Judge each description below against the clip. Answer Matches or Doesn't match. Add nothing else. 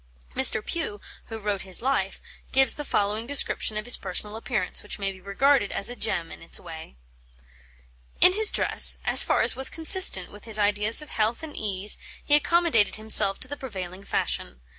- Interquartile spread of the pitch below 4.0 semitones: Doesn't match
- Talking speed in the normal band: Matches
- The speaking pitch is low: Doesn't match